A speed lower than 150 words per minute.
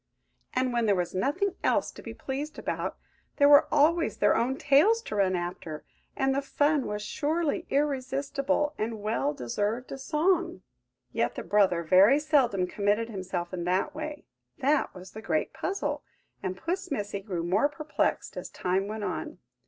No: average, 165 wpm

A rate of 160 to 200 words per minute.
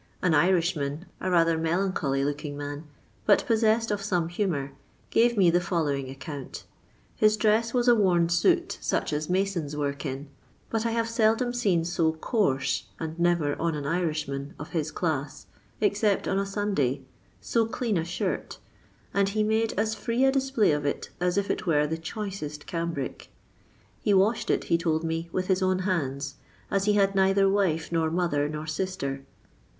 Yes: average, 175 wpm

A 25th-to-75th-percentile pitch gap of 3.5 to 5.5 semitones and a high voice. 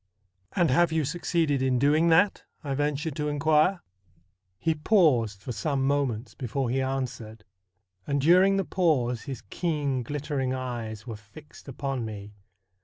No: average, 4.3 semitones; medium, 140 Hz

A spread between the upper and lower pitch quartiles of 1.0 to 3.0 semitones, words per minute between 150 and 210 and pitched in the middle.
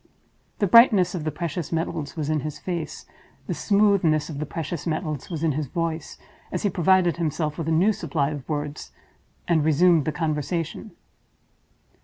Yes: narrow, 2.6 semitones; average, 170 wpm; medium, 160 Hz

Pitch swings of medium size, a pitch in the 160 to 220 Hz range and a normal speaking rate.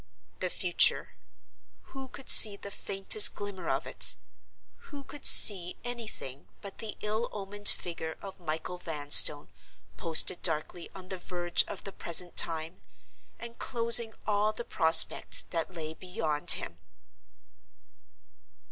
No: average, 4.4 semitones; medium, 185 Hz; slow, 125 wpm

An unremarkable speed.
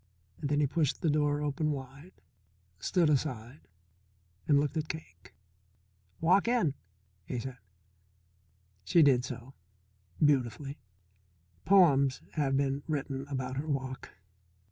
No: slow, 115 wpm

